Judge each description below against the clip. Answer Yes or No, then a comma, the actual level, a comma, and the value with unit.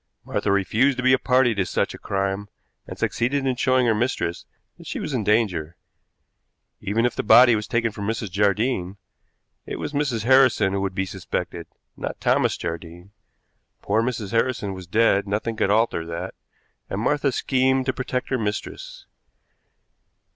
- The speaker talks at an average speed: Yes, average, 170 wpm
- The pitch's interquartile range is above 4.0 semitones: Yes, average, 4.6 semitones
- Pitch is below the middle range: Yes, low, 110 Hz